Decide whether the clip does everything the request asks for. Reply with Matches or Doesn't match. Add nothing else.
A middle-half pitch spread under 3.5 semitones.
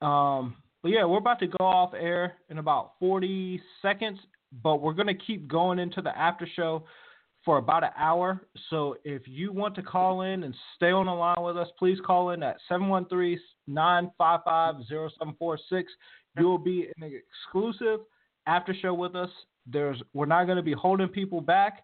Matches